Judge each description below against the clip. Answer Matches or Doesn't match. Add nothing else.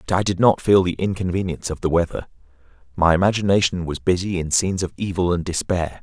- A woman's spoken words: Doesn't match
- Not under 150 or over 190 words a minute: Doesn't match